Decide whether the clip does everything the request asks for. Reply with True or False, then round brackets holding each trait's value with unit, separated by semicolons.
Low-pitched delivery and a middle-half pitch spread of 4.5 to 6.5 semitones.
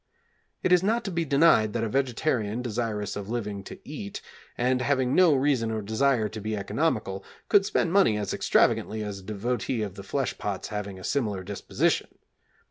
True (115 Hz; 5.1 semitones)